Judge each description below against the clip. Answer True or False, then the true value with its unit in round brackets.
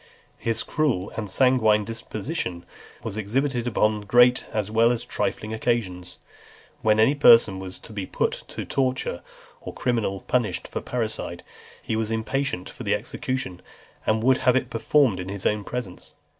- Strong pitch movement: False (3.6 semitones)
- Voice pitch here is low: True (110 Hz)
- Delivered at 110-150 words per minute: False (165 wpm)